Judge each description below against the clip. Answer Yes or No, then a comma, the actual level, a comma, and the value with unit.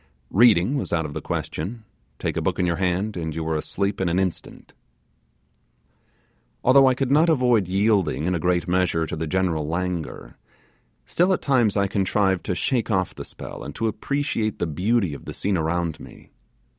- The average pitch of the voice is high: No, very low, 95 Hz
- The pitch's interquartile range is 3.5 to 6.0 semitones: Yes, average, 5.0 semitones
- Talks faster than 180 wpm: Yes, average, 190 wpm